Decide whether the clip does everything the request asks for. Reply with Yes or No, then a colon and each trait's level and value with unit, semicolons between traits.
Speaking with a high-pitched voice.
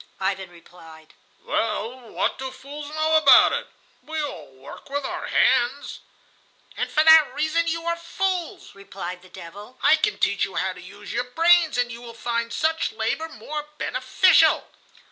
Yes: very high, 260 Hz